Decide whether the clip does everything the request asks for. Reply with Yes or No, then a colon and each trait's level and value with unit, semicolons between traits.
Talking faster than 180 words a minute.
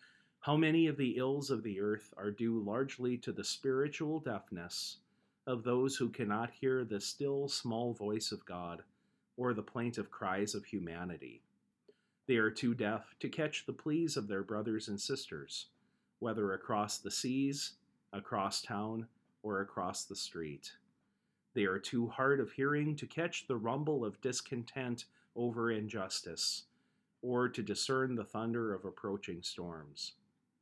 No: average, 150 wpm